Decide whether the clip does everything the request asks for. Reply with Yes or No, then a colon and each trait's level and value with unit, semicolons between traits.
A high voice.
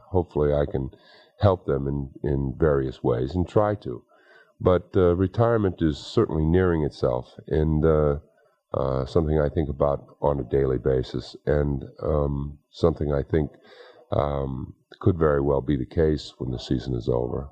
No: very low, 75 Hz